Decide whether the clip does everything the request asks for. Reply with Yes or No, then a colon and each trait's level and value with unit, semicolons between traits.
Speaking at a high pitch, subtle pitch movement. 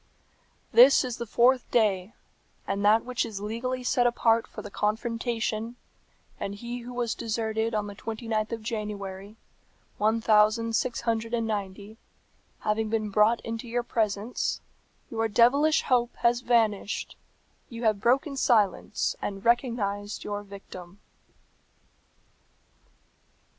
Yes: high, 225 Hz; narrow, 2.2 semitones